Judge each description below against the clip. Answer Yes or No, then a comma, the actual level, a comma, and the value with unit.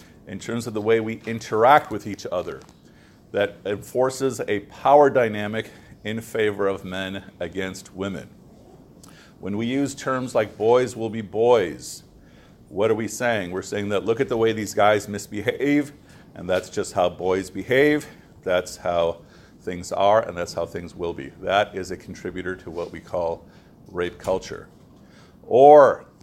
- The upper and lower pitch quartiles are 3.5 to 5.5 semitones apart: Yes, average, 4.1 semitones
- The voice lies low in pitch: Yes, low, 105 Hz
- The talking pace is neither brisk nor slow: Yes, average, 160 wpm